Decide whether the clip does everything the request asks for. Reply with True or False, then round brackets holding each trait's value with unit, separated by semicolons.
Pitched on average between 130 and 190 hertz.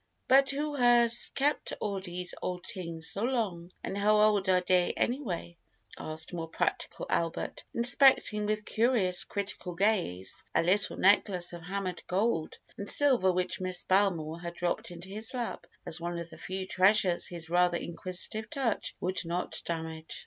True (185 Hz)